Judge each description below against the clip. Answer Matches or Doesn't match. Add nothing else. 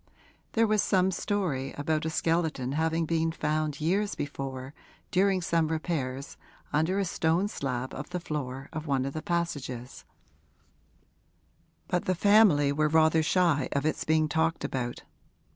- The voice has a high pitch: Doesn't match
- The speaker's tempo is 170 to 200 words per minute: Doesn't match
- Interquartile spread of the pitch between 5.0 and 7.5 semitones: Doesn't match